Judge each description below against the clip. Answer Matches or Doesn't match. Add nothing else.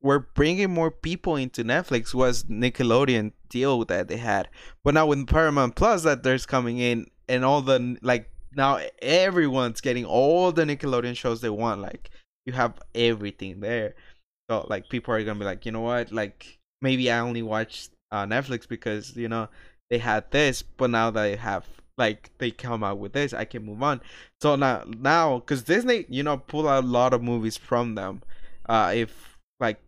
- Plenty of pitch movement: Doesn't match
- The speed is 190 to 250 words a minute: Matches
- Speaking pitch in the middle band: Doesn't match